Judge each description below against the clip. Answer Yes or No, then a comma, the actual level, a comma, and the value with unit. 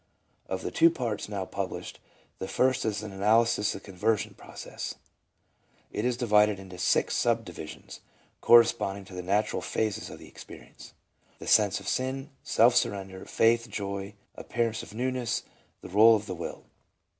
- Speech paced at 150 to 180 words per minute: Yes, average, 160 wpm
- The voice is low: Yes, low, 105 Hz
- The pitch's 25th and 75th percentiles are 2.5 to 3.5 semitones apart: Yes, average, 3.2 semitones